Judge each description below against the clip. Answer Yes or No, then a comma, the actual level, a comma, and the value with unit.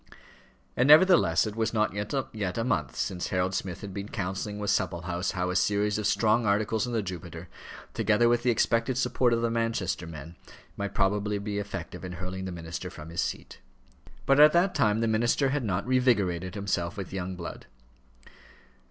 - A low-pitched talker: Yes, low, 105 Hz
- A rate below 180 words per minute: No, average, 185 wpm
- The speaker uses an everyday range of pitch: Yes, average, 3.9 semitones